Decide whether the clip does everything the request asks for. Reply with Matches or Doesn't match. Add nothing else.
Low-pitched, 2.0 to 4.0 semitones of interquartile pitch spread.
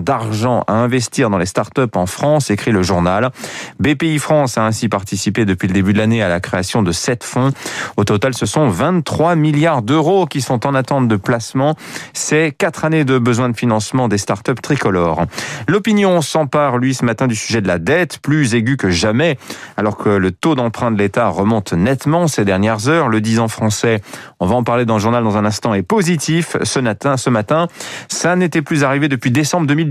Doesn't match